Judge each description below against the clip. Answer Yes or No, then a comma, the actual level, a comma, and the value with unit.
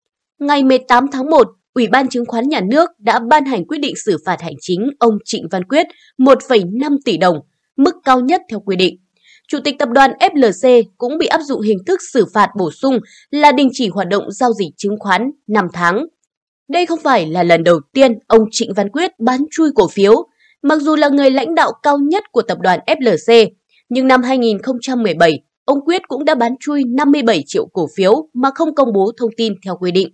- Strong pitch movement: Yes, wide, 6.0 semitones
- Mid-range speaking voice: No, very high, 255 Hz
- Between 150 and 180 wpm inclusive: No, average, 215 wpm